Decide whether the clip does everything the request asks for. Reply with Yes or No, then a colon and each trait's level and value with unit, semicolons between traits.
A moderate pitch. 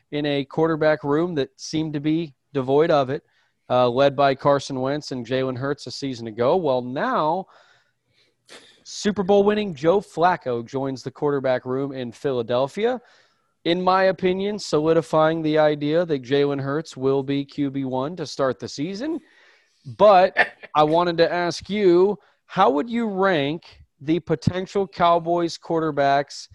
Yes: medium, 150 Hz